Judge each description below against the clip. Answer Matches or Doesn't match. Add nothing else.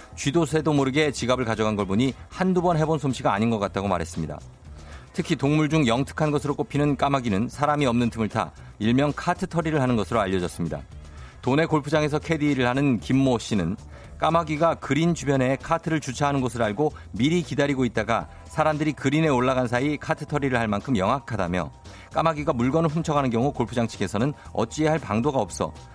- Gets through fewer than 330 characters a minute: Doesn't match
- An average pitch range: Doesn't match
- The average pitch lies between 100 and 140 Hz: Matches